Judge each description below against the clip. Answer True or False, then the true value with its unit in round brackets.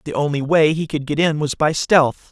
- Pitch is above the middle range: False (155 Hz)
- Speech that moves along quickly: True (260 wpm)